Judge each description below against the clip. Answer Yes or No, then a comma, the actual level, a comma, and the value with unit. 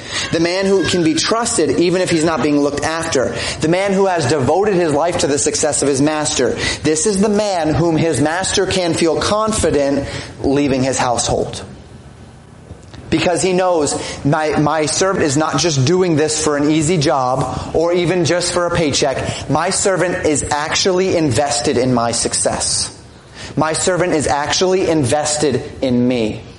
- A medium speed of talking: Yes, average, 170 wpm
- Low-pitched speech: No, medium, 155 Hz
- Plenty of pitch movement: No, average, 4.0 semitones